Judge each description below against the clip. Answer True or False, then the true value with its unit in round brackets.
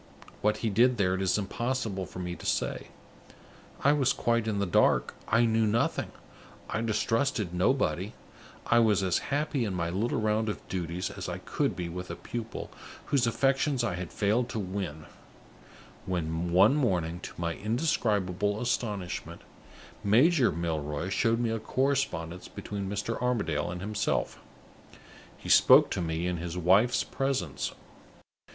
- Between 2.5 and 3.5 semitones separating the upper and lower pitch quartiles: False (4.8 semitones)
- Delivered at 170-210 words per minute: False (155 wpm)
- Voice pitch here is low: True (105 Hz)